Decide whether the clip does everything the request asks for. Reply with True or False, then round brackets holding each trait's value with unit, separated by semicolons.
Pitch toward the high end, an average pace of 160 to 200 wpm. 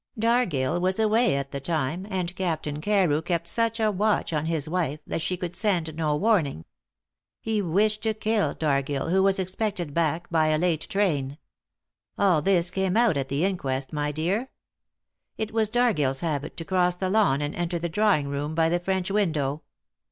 False (175 Hz; 180 wpm)